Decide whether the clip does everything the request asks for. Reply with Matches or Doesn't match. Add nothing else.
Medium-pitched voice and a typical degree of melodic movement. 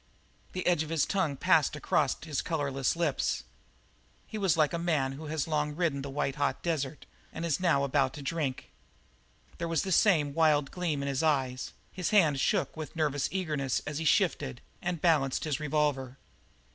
Matches